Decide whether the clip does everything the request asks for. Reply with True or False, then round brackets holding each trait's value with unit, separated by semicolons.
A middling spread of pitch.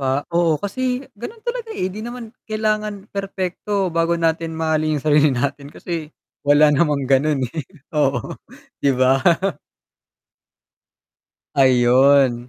False (6.0 semitones)